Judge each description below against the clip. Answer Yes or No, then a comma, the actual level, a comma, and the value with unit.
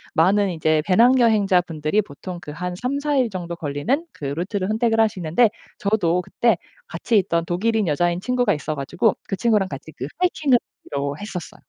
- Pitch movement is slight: No, wide, 5.4 semitones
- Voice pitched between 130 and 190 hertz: Yes, medium, 185 Hz